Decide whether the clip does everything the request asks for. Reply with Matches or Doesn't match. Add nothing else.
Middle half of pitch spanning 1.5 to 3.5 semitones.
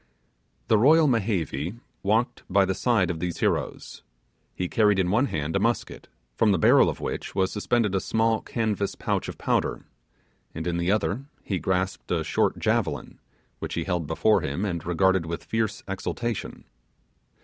Doesn't match